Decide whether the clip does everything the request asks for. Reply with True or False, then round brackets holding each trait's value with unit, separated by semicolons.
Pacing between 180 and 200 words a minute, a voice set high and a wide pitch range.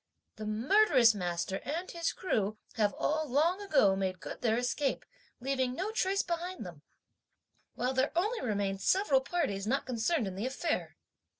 False (160 wpm; 260 Hz; 8.3 semitones)